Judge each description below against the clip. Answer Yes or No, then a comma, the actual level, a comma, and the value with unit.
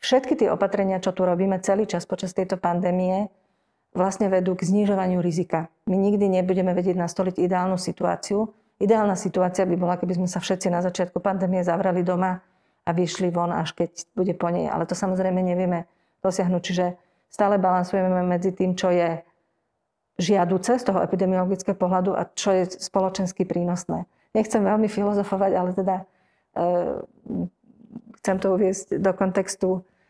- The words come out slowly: No, average, 155 wpm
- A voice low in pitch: No, medium, 185 Hz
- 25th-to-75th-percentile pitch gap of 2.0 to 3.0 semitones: No, narrow, 1.3 semitones